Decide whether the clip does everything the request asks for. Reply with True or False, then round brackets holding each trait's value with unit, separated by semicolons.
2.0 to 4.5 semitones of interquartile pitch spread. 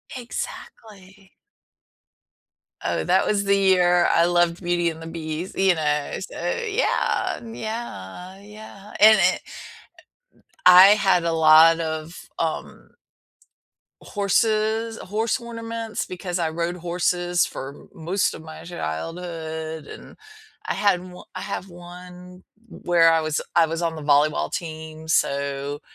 True (3.7 semitones)